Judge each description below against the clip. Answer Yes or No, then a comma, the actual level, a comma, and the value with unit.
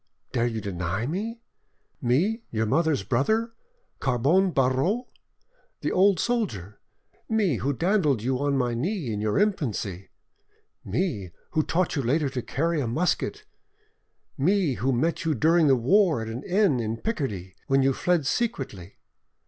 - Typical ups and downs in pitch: No, wide, 7.6 semitones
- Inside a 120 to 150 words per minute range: Yes, average, 145 wpm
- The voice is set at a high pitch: No, medium, 140 Hz